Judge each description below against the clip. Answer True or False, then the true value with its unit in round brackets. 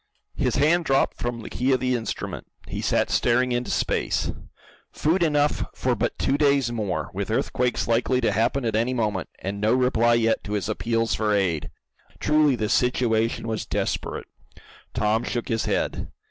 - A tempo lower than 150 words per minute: False (175 wpm)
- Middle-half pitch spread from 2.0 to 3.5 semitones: True (2.8 semitones)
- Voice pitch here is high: False (120 Hz)